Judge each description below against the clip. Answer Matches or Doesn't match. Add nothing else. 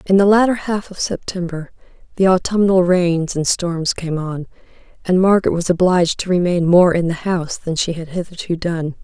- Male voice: Doesn't match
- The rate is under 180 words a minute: Doesn't match